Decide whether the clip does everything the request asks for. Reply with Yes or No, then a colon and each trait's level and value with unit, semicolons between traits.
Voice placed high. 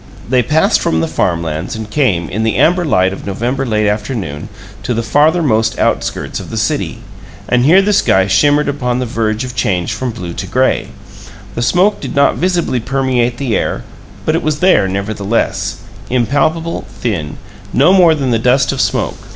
No: low, 120 Hz